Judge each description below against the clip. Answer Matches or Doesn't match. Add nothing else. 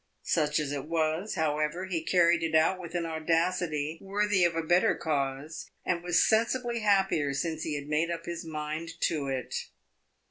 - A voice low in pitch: Doesn't match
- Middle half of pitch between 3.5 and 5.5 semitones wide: Doesn't match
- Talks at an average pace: Matches